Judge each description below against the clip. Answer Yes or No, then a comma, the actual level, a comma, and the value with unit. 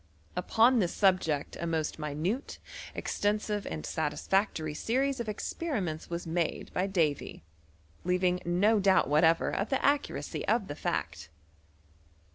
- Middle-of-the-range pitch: Yes, medium, 180 Hz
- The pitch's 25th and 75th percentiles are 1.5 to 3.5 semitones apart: No, average, 4.9 semitones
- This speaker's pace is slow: Yes, slow, 125 wpm